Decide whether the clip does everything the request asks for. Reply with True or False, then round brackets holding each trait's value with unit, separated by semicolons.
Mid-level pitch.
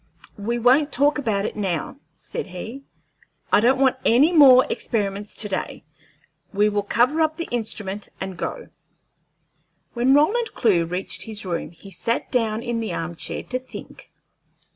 False (230 Hz)